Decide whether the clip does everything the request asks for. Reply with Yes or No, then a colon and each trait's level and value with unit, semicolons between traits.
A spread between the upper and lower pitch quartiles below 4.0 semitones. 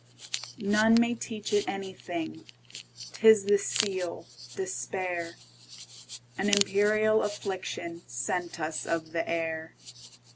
No: average, 4.4 semitones